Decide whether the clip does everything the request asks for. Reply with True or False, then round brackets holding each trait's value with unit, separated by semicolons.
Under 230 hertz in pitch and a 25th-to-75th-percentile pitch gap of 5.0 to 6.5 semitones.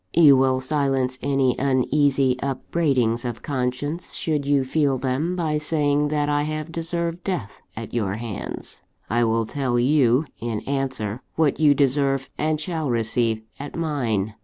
False (135 Hz; 3.3 semitones)